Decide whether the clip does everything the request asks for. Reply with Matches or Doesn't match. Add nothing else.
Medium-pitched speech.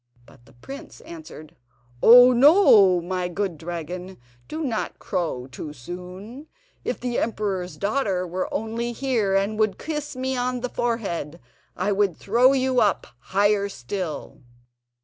Doesn't match